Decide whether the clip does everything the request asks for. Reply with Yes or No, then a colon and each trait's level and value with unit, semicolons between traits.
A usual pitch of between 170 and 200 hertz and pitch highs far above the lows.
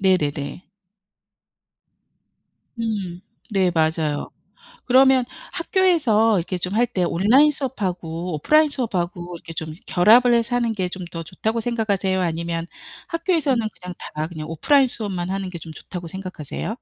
Yes: high, 190 Hz; wide, 5.8 semitones